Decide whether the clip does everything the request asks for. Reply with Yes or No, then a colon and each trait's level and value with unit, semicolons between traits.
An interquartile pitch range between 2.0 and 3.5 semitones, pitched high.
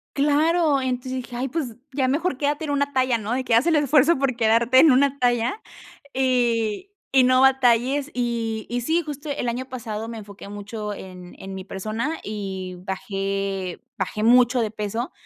No: average, 4.2 semitones; high, 245 Hz